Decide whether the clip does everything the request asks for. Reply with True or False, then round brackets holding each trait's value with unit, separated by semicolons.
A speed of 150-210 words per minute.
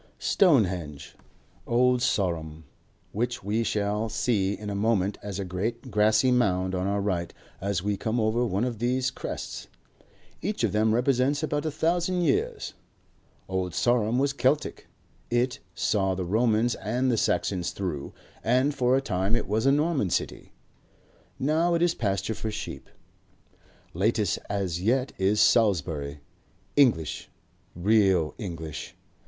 False (140 wpm)